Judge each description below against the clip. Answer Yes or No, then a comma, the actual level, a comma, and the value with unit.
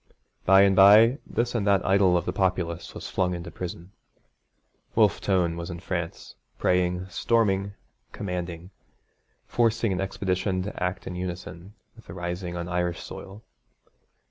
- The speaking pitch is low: Yes, very low, 90 Hz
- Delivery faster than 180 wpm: No, average, 145 wpm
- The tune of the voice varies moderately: No, narrow, 2.1 semitones